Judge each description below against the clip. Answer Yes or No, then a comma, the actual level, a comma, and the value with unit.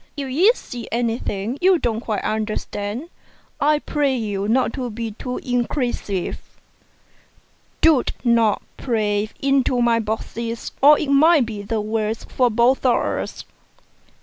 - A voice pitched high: Yes, high, 235 Hz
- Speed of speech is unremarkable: No, slow, 130 wpm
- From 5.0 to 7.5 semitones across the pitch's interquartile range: No, average, 3.9 semitones